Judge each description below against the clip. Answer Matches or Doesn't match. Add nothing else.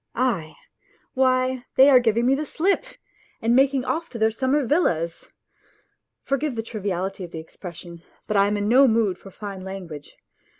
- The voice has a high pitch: Matches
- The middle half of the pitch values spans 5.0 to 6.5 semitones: Matches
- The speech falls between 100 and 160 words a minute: Doesn't match